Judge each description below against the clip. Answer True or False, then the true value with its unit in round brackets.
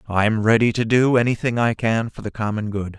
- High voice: False (110 Hz)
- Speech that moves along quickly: True (220 wpm)